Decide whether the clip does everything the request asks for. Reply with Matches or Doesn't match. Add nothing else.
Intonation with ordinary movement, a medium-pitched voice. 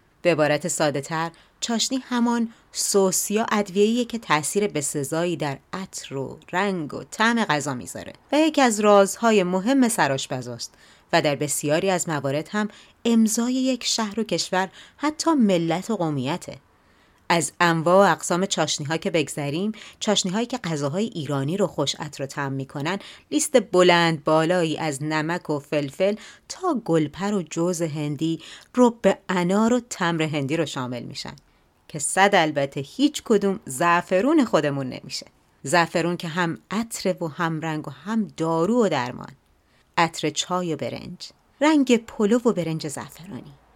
Doesn't match